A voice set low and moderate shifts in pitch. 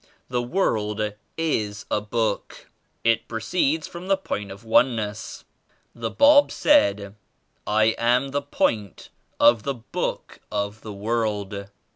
Yes: low, 110 Hz; average, 4.5 semitones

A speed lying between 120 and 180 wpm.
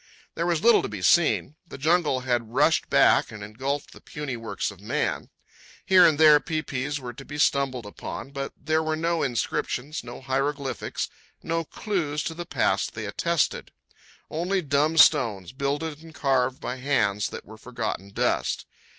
Yes: average, 165 wpm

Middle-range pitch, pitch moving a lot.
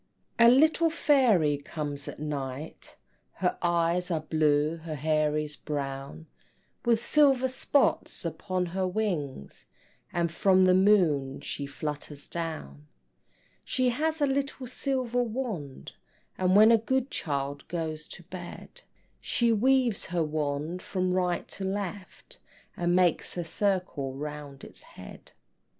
Yes: medium, 175 Hz; wide, 6.8 semitones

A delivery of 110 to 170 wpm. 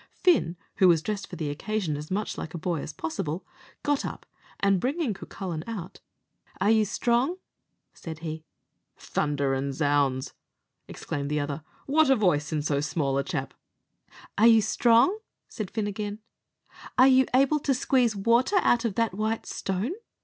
Yes: average, 165 wpm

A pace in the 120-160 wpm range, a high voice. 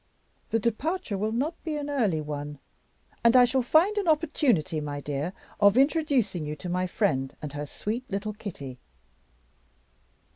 Yes: average, 155 wpm; high, 210 Hz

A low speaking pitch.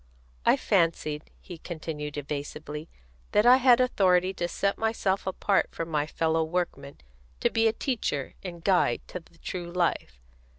No: medium, 175 Hz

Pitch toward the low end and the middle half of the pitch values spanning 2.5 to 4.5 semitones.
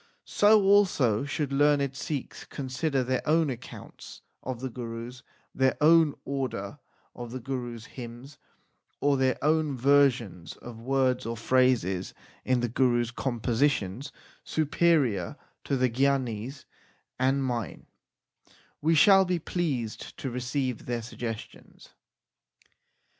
Yes: low, 130 Hz; average, 3.1 semitones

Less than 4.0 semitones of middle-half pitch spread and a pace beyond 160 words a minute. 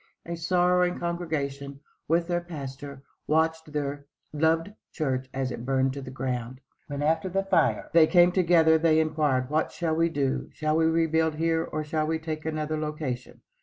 Yes: average, 2.8 semitones; average, 170 wpm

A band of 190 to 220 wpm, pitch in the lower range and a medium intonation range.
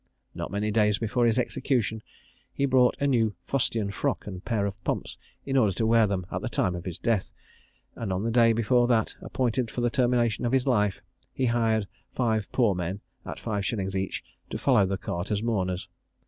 Yes: fast, 205 wpm; low, 110 Hz; average, 3.3 semitones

